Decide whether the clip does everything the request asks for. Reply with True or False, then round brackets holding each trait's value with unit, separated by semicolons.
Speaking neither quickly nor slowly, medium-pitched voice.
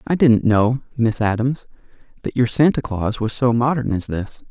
False (185 wpm; 120 Hz)